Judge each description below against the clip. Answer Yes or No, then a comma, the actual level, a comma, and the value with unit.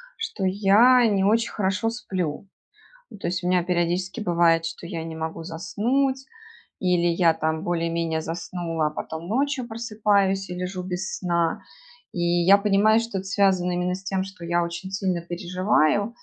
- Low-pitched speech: No, medium, 185 Hz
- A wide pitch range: No, average, 2.9 semitones